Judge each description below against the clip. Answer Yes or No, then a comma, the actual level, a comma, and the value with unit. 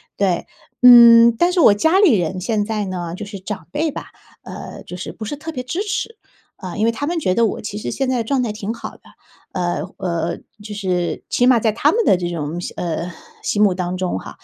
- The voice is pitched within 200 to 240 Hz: Yes, high, 210 Hz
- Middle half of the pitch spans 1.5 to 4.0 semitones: No, wide, 5.6 semitones